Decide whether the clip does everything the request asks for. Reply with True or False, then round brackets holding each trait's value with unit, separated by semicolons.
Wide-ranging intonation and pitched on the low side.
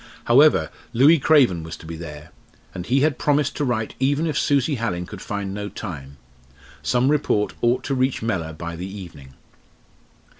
True (7.9 semitones; 110 Hz)